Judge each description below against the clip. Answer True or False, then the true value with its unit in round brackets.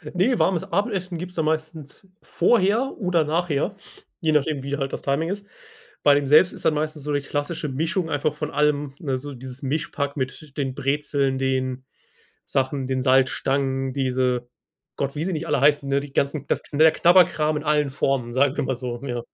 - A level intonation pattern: False (3.1 semitones)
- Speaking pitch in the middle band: True (145 Hz)